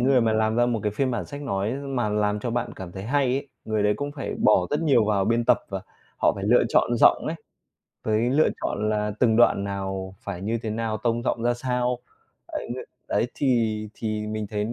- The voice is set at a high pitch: No, low, 110 Hz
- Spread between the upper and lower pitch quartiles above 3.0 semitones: No, average, 2.7 semitones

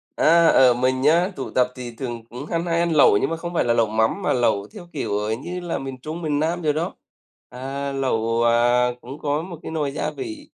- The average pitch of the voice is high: No, medium, 140 Hz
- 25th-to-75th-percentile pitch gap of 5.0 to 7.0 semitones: Yes, wide, 5.4 semitones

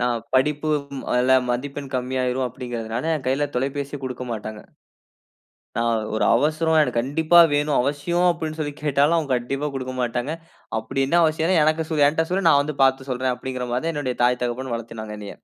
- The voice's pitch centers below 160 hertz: Yes, low, 135 Hz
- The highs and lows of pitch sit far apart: No, average, 3.6 semitones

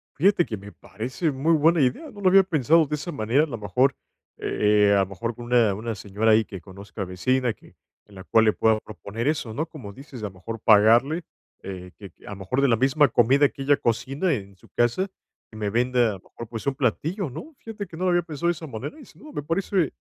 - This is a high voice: No, low, 125 Hz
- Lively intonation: Yes, wide, 6.6 semitones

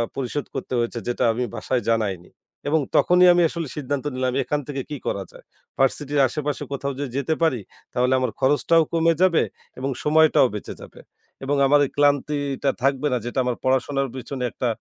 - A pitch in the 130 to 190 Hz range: Yes, medium, 140 Hz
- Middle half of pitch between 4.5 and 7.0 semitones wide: No, narrow, 2.6 semitones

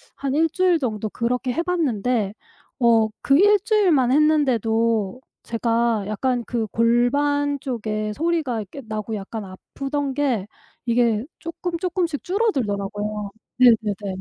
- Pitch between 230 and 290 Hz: Yes, high, 245 Hz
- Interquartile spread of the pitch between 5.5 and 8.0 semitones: No, average, 5.1 semitones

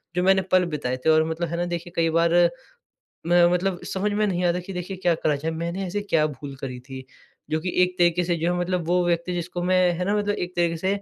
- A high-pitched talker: No, medium, 175 Hz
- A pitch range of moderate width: No, narrow, 1.7 semitones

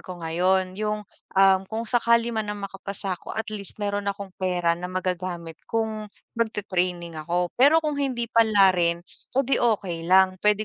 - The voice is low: No, high, 195 Hz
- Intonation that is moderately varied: Yes, average, 3.3 semitones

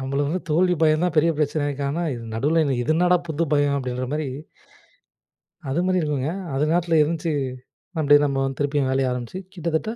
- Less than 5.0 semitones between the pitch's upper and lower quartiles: Yes, average, 3.1 semitones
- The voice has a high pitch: No, medium, 150 Hz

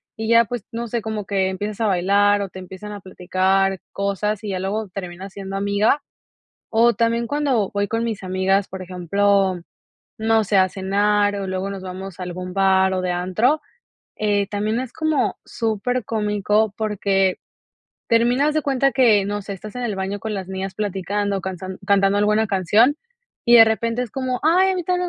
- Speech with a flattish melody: No, average, 3.0 semitones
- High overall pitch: Yes, high, 205 Hz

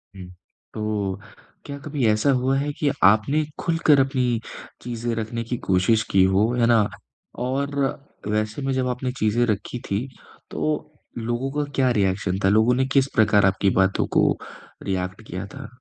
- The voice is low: Yes, low, 115 Hz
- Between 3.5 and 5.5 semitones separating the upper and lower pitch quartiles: Yes, average, 4.6 semitones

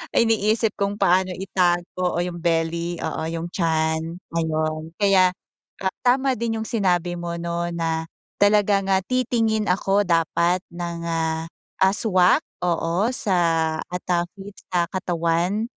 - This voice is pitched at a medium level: Yes, medium, 180 Hz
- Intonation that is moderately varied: Yes, average, 3.2 semitones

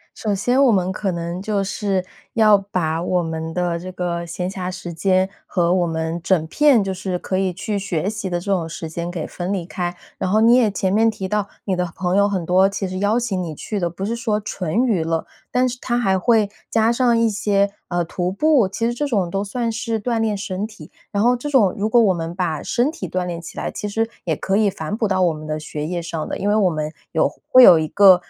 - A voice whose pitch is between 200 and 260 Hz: No, high, 190 Hz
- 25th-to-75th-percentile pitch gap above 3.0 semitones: Yes, average, 3.6 semitones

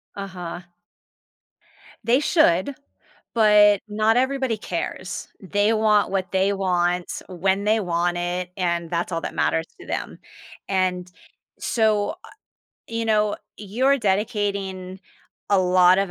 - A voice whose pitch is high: Yes, high, 195 Hz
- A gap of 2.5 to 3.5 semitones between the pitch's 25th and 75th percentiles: Yes, average, 3.0 semitones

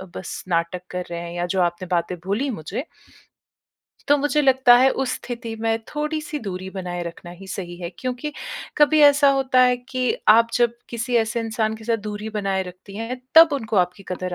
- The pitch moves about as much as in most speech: No, wide, 5.9 semitones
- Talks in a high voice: Yes, high, 225 Hz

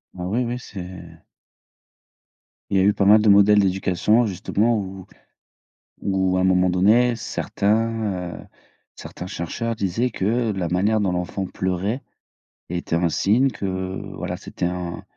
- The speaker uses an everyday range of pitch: Yes, average, 3.2 semitones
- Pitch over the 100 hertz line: No, very low, 95 Hz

